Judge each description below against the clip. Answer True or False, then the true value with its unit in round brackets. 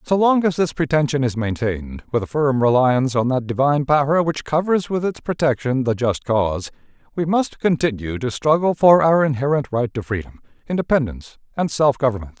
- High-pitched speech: False (135 Hz)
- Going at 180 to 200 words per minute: True (185 wpm)